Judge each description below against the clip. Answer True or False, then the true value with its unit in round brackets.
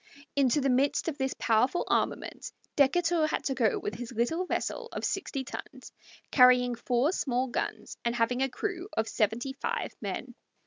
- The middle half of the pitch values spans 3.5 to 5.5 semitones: True (3.8 semitones)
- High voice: True (265 Hz)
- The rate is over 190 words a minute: False (170 wpm)